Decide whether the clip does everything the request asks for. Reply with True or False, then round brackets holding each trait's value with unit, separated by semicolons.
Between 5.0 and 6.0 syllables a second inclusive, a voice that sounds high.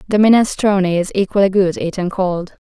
True (5.5 syllables/s; 195 Hz)